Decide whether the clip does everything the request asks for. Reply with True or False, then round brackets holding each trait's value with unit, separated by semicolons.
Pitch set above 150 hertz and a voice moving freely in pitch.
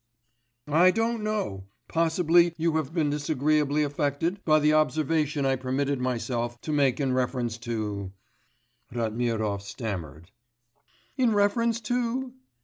False (145 Hz; 5.8 semitones)